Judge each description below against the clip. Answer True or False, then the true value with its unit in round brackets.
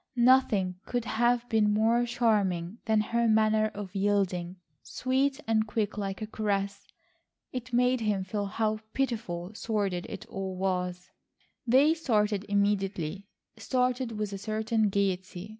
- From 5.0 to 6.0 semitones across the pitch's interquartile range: False (3.3 semitones)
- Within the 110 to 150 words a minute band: True (135 wpm)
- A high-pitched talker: True (215 Hz)